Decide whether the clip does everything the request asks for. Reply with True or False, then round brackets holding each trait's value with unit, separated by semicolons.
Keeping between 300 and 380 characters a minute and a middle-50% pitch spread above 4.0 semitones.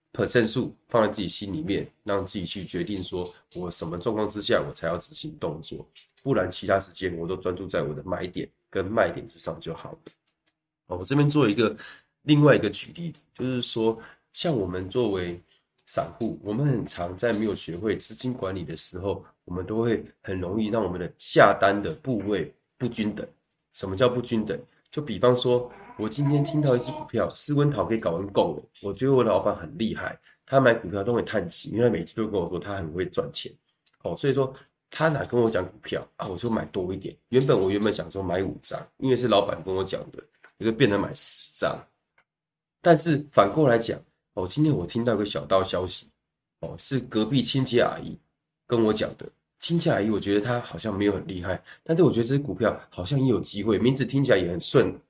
True (305 characters per minute; 5.6 semitones)